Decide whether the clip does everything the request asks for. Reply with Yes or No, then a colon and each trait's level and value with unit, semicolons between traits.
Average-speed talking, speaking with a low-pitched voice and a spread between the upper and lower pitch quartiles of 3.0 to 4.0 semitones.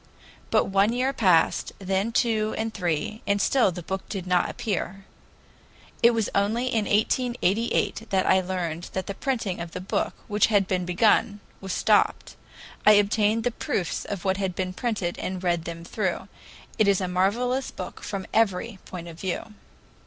No: average, 175 wpm; high, 195 Hz; average, 3.3 semitones